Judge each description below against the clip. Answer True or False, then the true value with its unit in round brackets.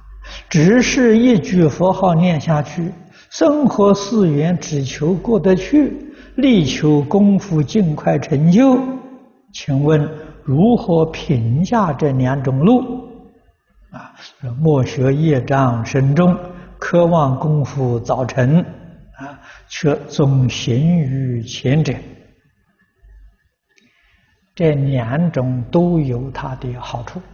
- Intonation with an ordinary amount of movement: False (6.1 semitones)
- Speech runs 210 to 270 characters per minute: False (145 characters per minute)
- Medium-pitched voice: True (160 Hz)